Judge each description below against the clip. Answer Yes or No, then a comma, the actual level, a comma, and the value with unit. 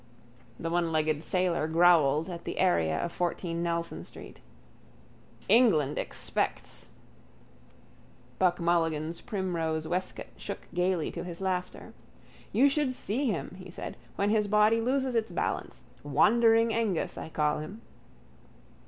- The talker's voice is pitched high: No, medium, 175 Hz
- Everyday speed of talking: No, slow, 125 wpm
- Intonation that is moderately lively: Yes, average, 4.9 semitones